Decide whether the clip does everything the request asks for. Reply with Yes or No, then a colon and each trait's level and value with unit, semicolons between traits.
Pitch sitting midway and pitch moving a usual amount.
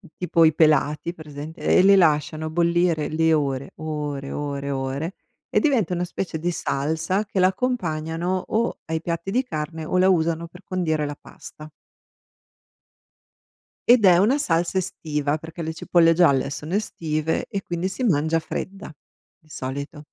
Yes: medium, 160 Hz; average, 3.1 semitones